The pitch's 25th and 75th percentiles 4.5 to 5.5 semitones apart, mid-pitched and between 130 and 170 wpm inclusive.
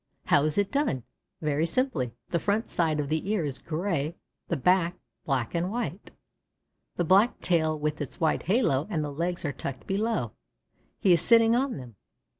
No: average, 5.2 semitones; medium, 165 Hz; average, 180 wpm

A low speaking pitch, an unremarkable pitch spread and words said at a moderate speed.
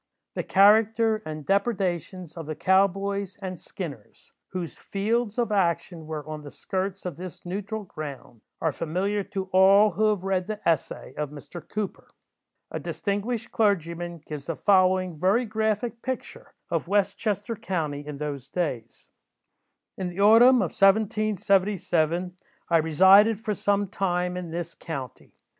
No: high, 190 Hz; average, 3.7 semitones; average, 150 wpm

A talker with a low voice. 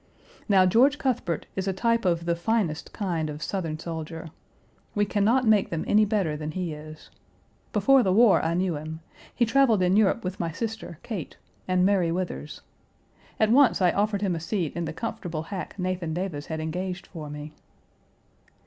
No: medium, 185 Hz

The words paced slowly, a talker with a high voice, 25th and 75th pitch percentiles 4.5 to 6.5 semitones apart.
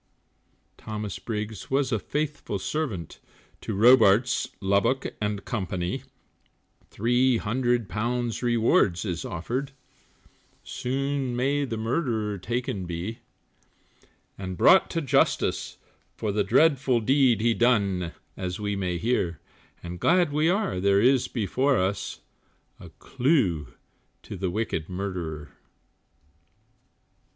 No: slow, 110 wpm; low, 110 Hz; average, 5.2 semitones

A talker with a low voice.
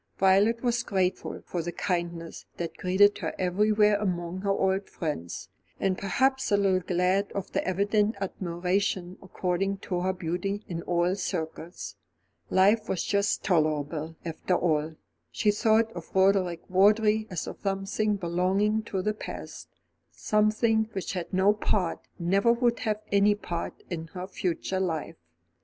No: high, 190 Hz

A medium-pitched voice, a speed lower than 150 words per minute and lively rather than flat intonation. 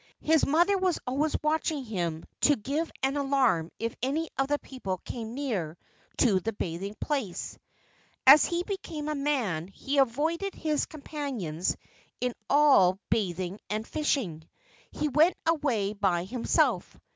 No: very high, 270 Hz; average, 140 wpm; wide, 7.2 semitones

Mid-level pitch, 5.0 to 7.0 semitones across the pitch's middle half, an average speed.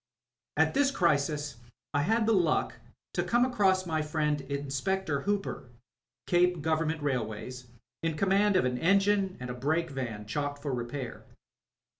Yes: medium, 155 Hz; wide, 5.5 semitones; average, 145 wpm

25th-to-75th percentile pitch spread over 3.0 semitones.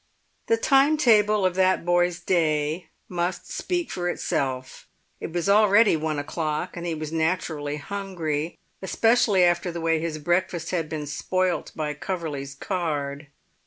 Yes: average, 3.5 semitones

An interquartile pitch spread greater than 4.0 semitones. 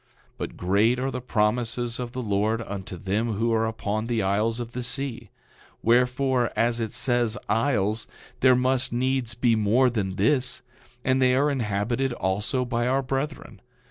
No: average, 2.8 semitones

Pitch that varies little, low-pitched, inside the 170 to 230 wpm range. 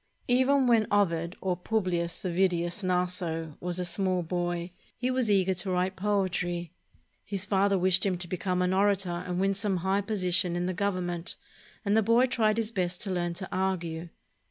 No: narrow, 2.3 semitones; medium, 185 Hz; average, 180 wpm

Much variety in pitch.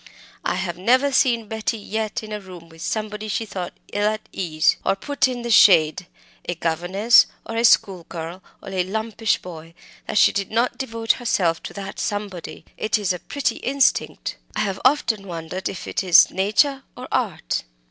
No: average, 4.0 semitones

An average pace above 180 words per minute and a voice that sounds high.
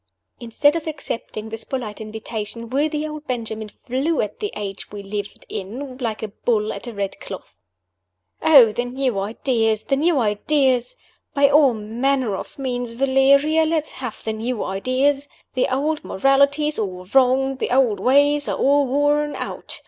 No: average, 165 wpm; very high, 255 Hz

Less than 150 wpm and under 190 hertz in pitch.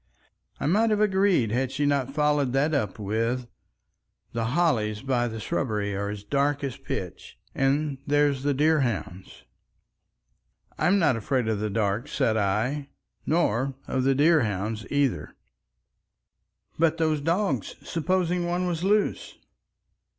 Yes: average, 140 wpm; low, 135 Hz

